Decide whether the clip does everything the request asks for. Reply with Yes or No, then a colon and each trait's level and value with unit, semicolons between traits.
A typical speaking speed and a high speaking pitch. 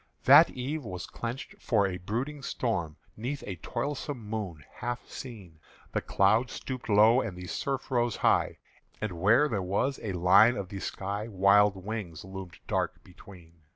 No: average, 160 wpm; low, 105 Hz